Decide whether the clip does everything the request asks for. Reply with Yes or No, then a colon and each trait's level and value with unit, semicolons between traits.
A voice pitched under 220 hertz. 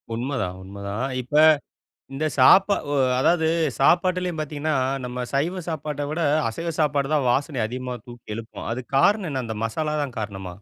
Yes: medium, 140 Hz